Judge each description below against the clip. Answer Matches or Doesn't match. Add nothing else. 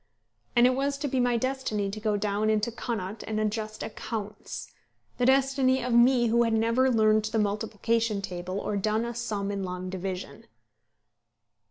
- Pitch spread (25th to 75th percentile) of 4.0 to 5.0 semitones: Doesn't match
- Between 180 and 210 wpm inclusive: Doesn't match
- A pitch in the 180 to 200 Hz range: Doesn't match